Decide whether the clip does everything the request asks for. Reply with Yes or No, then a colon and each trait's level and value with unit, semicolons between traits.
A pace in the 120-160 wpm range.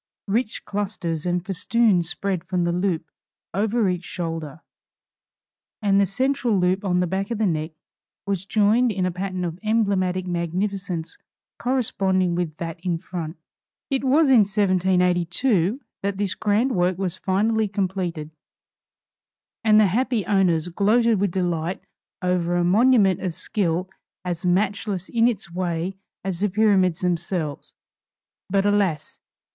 Yes: average, 140 wpm